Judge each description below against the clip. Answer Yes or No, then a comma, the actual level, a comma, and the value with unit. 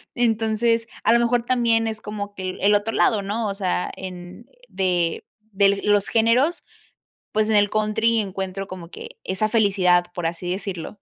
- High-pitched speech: Yes, high, 205 Hz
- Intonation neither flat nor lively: Yes, average, 3.2 semitones